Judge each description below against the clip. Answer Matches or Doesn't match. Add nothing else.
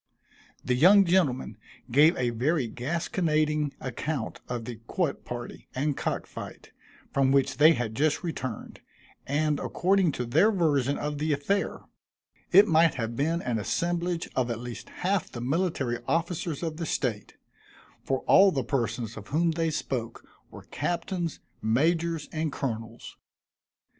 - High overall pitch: Doesn't match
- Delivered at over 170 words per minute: Doesn't match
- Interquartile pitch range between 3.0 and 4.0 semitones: Doesn't match